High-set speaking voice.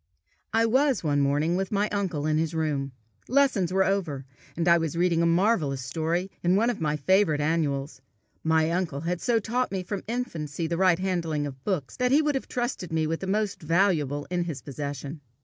No: medium, 170 Hz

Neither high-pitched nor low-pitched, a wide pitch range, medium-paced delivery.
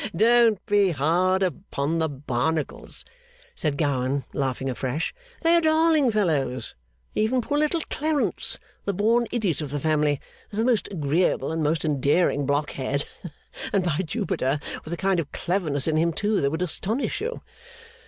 Yes: medium, 165 Hz; wide, 6.9 semitones; average, 155 wpm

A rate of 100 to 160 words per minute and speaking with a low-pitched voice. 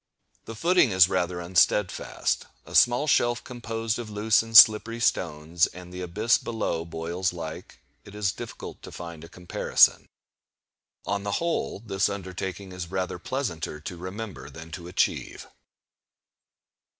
Yes: average, 140 wpm; very low, 95 Hz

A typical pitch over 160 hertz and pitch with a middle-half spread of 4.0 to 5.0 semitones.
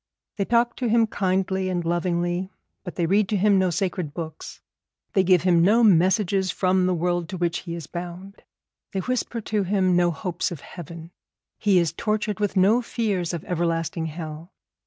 No: medium, 185 Hz; narrow, 2.6 semitones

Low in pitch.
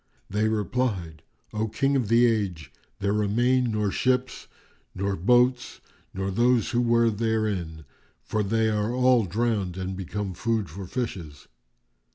Yes: low, 110 Hz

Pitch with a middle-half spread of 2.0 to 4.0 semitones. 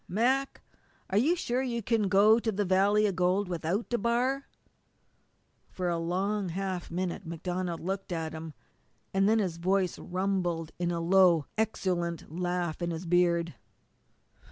Yes: average, 3.2 semitones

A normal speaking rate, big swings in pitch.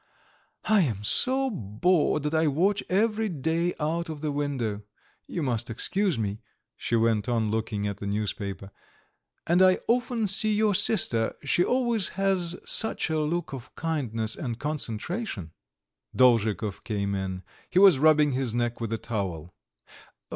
Yes: average, 155 wpm; wide, 8.7 semitones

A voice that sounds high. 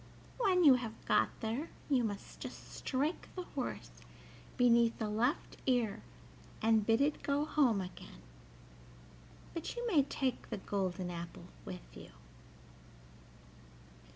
Yes: high, 240 Hz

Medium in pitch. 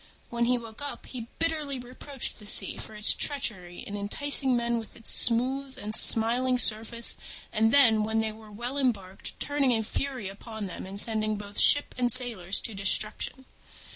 No: high, 230 Hz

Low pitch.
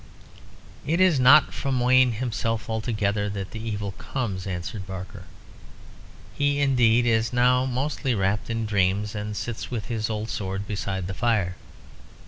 Yes: low, 110 Hz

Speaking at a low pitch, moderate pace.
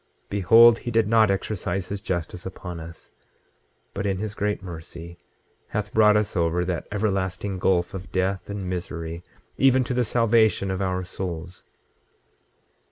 Yes: very low, 95 Hz; average, 150 wpm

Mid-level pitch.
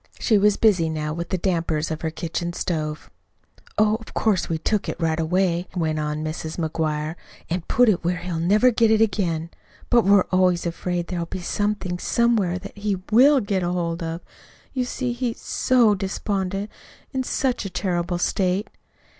Yes: medium, 180 Hz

